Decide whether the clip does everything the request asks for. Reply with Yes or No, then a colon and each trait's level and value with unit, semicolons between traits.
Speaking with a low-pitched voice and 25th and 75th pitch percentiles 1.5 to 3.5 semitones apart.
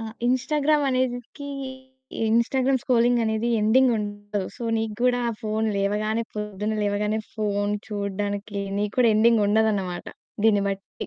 No: high, 215 Hz; average, 2.8 semitones